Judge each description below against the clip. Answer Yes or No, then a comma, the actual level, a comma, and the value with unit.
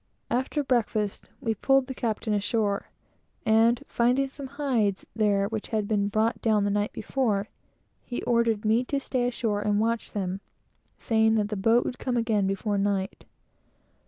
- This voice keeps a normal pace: Yes, average, 160 wpm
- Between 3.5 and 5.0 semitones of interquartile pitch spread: No, average, 2.8 semitones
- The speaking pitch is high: Yes, high, 220 Hz